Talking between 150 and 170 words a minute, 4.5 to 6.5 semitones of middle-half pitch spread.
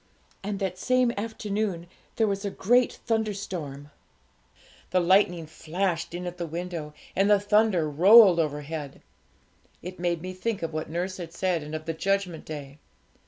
No: average, 160 wpm; average, 3.7 semitones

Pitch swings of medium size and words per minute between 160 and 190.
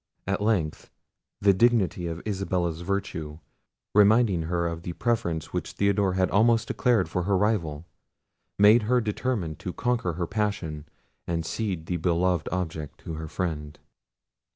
No: average, 4.0 semitones; average, 145 wpm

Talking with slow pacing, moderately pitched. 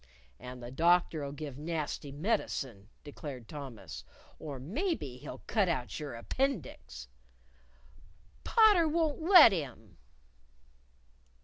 Yes: slow, 100 wpm; medium, 150 Hz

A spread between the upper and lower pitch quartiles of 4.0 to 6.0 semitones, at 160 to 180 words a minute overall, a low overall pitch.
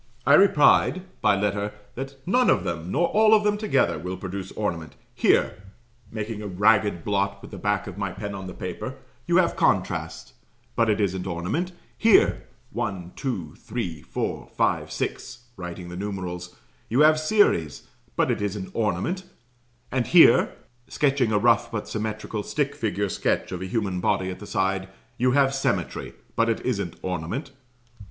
Yes: wide, 5.5 semitones; average, 165 wpm; low, 105 Hz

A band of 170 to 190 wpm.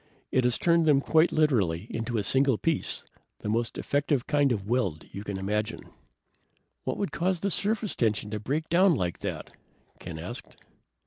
Yes: average, 175 wpm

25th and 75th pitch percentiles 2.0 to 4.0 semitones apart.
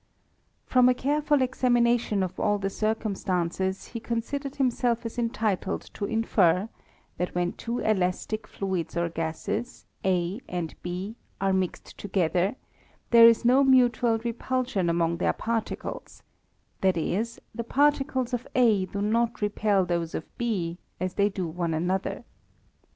No: average, 4.7 semitones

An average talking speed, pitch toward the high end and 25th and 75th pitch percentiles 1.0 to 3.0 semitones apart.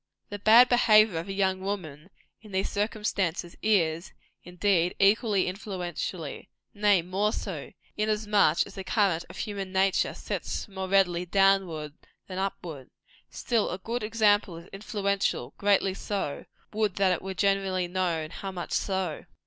Yes: average, 145 wpm; high, 195 Hz; narrow, 2.4 semitones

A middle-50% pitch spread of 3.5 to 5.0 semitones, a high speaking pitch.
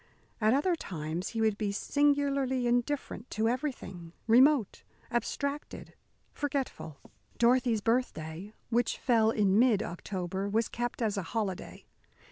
Yes: average, 4.4 semitones; high, 230 Hz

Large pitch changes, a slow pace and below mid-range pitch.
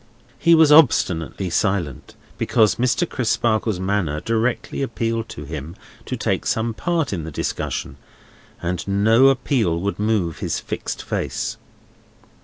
Yes: wide, 5.7 semitones; slow, 130 wpm; low, 110 Hz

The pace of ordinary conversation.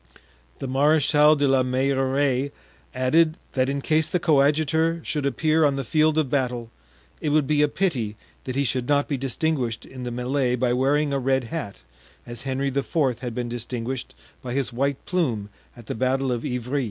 Yes: average, 185 wpm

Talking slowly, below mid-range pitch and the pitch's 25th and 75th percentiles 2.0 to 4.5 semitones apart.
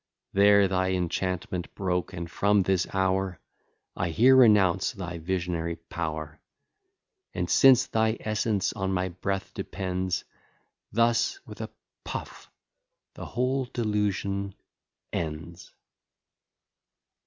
Yes: slow, 105 wpm; very low, 95 Hz; average, 2.8 semitones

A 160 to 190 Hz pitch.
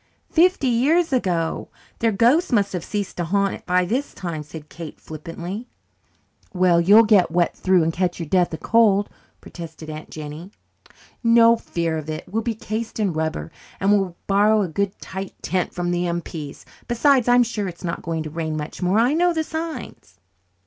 Yes: medium, 185 Hz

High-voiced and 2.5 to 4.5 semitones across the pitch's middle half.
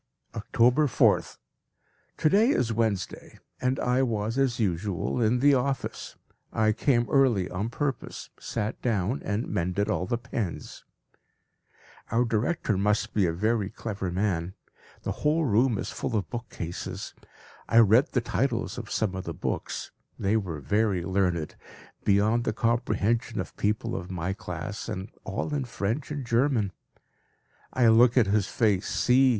No: low, 110 Hz; average, 3.9 semitones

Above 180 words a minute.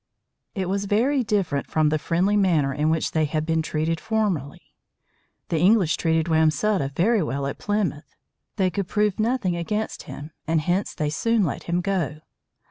No: average, 170 wpm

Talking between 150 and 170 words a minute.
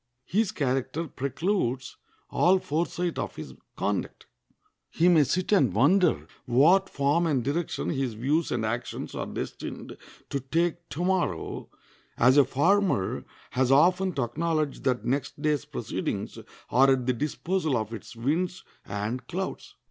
No: average, 140 wpm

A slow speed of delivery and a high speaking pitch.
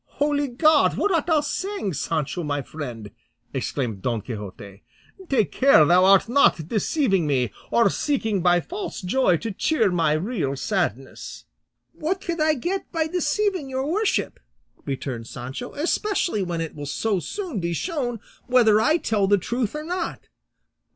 No: average, 155 wpm; high, 215 Hz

